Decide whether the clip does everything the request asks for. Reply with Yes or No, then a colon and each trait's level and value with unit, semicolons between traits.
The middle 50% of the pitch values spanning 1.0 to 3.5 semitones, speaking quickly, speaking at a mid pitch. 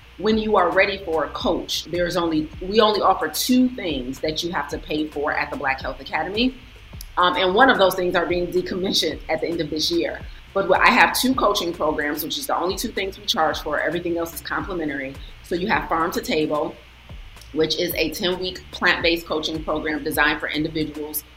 Yes: average, 3.2 semitones; fast, 215 wpm; medium, 165 Hz